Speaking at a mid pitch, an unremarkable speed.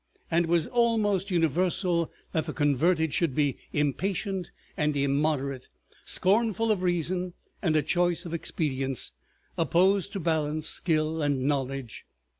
No: medium, 165 Hz; slow, 130 wpm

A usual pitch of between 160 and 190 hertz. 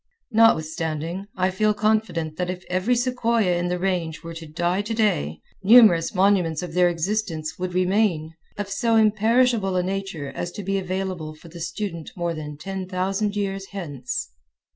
Yes: medium, 185 Hz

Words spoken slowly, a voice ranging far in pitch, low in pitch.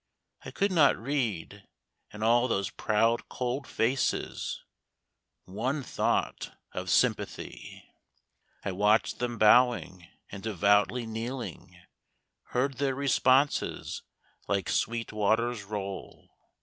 No: slow, 100 wpm; average, 3.7 semitones; low, 115 Hz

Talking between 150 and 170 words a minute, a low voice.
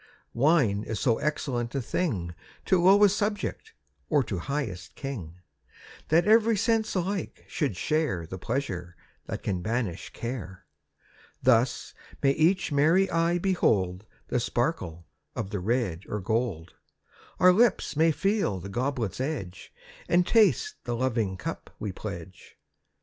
No: slow, 135 wpm; low, 125 Hz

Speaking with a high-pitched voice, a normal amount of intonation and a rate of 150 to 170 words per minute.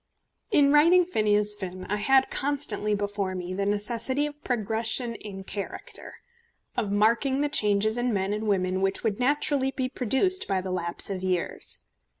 Yes: high, 215 Hz; average, 5.0 semitones; average, 160 wpm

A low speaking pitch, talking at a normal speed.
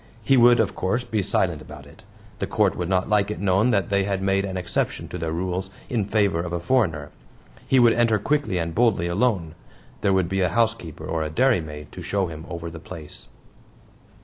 No: very low, 95 Hz; fast, 210 wpm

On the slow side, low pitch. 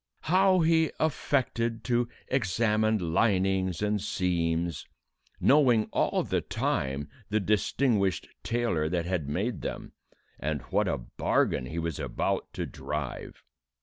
Yes: slow, 120 wpm; low, 100 Hz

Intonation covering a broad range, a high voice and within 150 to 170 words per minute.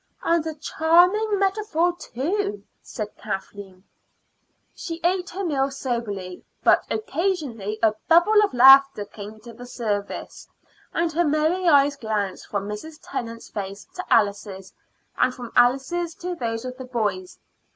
No: wide, 8.1 semitones; very high, 270 Hz; average, 140 wpm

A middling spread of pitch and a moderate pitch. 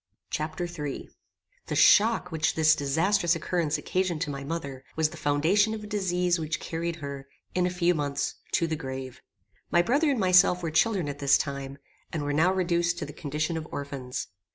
Yes: average, 3.7 semitones; medium, 160 Hz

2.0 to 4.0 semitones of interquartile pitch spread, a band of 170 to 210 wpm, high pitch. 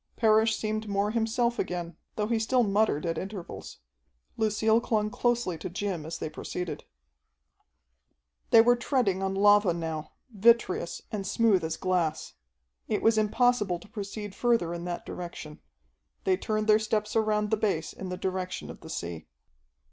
No: average, 3.7 semitones; average, 155 wpm; high, 205 Hz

